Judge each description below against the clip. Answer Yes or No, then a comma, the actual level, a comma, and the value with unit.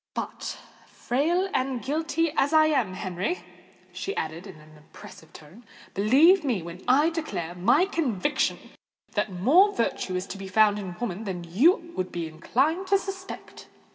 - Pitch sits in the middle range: No, high, 235 Hz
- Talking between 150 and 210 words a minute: Yes, average, 160 wpm